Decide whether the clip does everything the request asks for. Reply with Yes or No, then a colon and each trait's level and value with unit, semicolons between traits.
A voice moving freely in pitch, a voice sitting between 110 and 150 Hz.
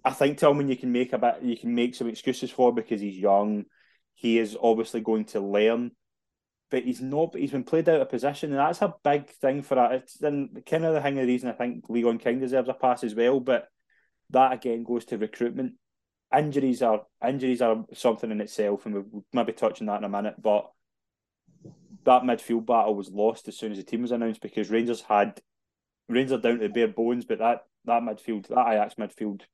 No: average, 2.8 semitones; low, 120 Hz